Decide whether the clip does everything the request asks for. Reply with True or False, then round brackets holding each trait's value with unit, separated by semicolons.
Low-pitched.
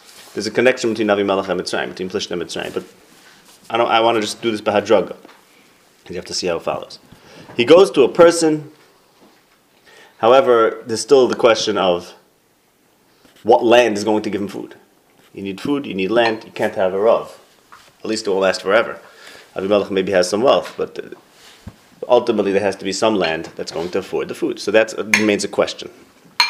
True (110 Hz)